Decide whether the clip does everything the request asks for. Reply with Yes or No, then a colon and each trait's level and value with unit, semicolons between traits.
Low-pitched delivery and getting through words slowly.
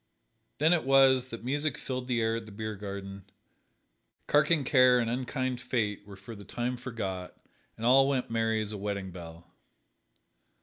No: low, 115 Hz; average, 170 wpm